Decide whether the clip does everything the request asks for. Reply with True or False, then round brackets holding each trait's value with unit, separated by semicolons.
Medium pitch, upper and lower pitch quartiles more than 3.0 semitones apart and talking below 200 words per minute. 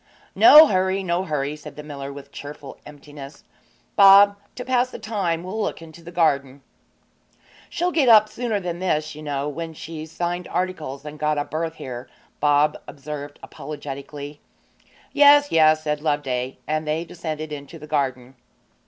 True (155 Hz; 3.8 semitones; 160 wpm)